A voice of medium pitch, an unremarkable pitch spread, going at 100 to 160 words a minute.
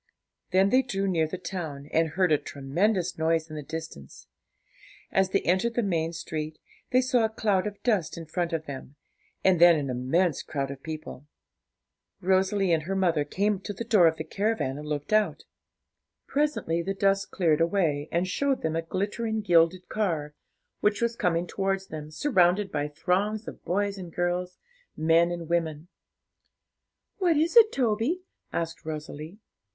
No: medium, 175 Hz; average, 4.3 semitones; average, 170 wpm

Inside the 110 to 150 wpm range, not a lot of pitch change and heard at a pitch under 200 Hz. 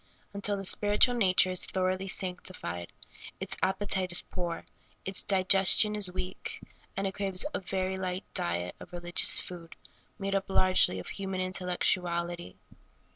Yes: average, 145 wpm; narrow, 1.5 semitones; medium, 185 Hz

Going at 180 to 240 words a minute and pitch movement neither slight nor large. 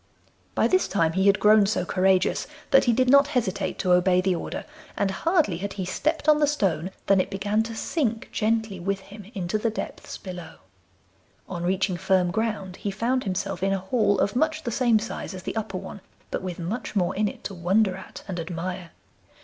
Yes: fast, 205 wpm; average, 3.3 semitones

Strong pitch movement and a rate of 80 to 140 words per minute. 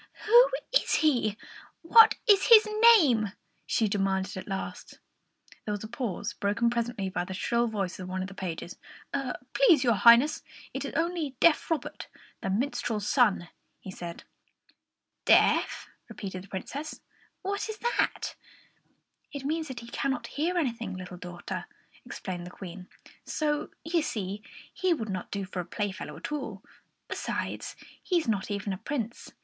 No: wide, 7.7 semitones; average, 155 wpm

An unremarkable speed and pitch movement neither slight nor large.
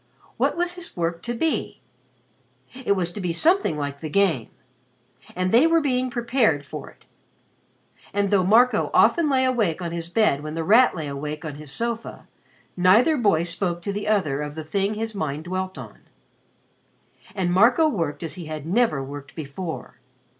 No: average, 175 wpm; wide, 6.7 semitones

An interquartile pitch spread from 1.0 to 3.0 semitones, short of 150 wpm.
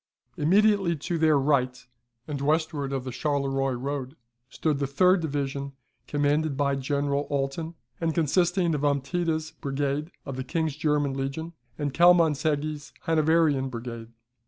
Yes: average, 2.7 semitones; slow, 135 wpm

